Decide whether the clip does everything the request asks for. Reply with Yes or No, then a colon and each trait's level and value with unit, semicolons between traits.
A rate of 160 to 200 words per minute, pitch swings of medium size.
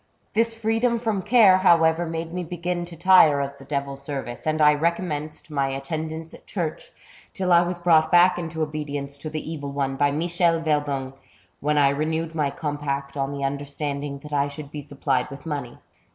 Yes: average, 190 wpm; average, 3.3 semitones